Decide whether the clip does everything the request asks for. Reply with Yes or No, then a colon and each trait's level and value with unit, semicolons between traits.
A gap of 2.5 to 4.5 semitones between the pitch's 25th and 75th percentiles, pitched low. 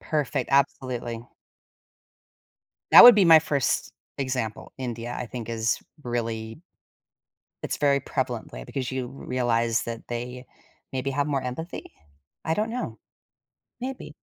Yes: average, 3.4 semitones; low, 130 Hz